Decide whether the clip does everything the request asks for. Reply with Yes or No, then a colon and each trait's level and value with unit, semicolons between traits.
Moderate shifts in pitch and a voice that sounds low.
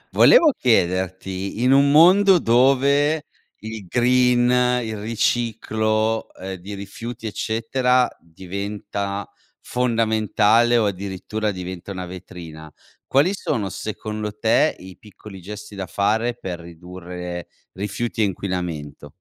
Yes: average, 4.3 semitones; low, 105 Hz